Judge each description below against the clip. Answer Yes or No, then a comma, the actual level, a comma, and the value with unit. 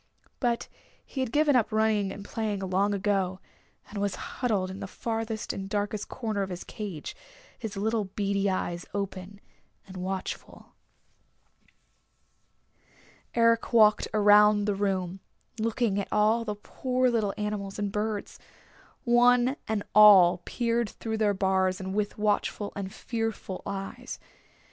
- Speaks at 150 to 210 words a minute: No, slow, 135 wpm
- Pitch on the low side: No, high, 205 Hz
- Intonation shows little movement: Yes, narrow, 2.3 semitones